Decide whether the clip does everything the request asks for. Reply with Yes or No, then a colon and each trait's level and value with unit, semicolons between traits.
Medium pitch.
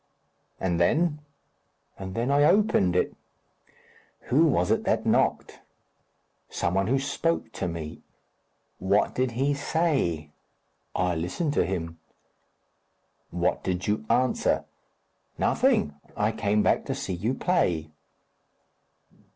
No: low, 105 Hz